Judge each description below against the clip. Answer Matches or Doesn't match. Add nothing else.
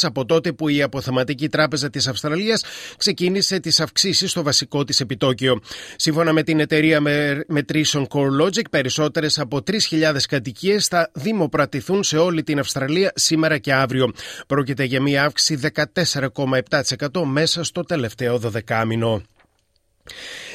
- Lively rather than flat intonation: Doesn't match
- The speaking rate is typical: Matches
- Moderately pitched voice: Matches